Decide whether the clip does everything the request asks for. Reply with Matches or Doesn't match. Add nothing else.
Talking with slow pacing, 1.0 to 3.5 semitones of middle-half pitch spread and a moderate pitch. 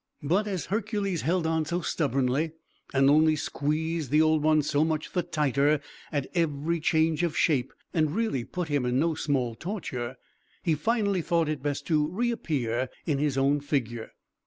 Doesn't match